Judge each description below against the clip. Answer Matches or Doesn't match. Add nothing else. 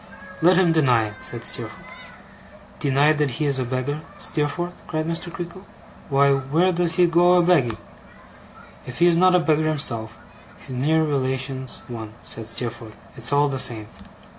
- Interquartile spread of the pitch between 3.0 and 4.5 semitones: Doesn't match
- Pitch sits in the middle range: Matches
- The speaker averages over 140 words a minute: Matches